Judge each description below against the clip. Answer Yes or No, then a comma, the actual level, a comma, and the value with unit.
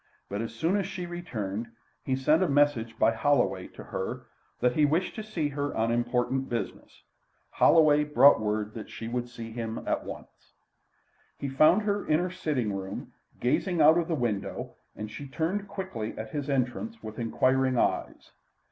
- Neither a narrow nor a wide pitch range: No, wide, 6.0 semitones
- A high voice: No, low, 135 Hz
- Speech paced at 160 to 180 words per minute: Yes, average, 175 wpm